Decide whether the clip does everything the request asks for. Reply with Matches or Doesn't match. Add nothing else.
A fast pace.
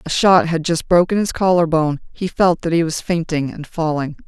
Matches